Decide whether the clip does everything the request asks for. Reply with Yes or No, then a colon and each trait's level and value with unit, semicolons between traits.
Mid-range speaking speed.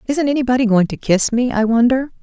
No: fast, 215 wpm